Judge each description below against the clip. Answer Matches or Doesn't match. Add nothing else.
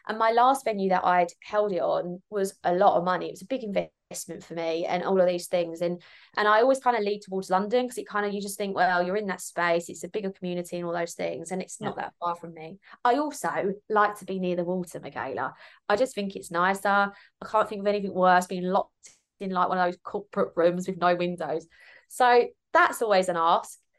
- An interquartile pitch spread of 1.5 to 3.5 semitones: Matches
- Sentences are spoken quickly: Matches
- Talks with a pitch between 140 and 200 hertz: Matches